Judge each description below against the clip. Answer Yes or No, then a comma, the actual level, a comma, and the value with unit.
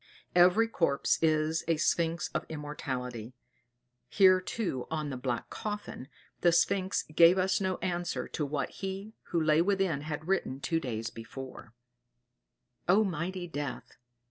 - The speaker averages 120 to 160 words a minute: Yes, average, 140 wpm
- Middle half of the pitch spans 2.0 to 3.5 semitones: No, average, 4.8 semitones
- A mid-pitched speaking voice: Yes, medium, 165 Hz